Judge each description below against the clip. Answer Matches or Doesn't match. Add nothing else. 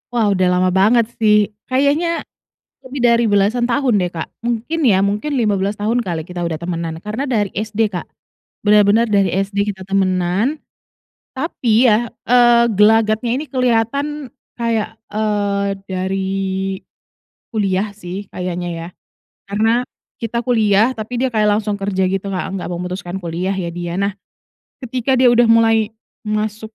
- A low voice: Doesn't match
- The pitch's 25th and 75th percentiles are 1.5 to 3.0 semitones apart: Doesn't match